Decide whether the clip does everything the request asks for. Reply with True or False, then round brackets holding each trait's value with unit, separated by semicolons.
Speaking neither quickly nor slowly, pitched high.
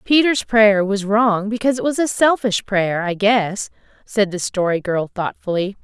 True (175 wpm; 210 Hz)